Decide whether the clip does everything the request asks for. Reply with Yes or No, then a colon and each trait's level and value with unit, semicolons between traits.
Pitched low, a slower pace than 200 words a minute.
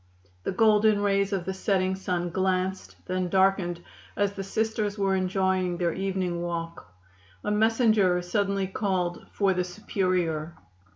No: high, 190 Hz; slow, 135 wpm